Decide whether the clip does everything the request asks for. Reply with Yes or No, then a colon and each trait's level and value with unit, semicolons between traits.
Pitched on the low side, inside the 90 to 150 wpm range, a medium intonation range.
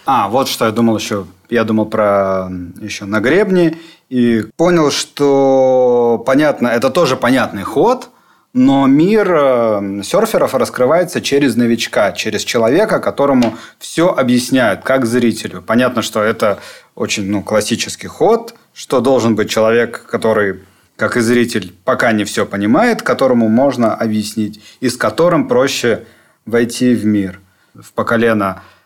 Yes: low, 115 Hz; average, 135 wpm; average, 3.4 semitones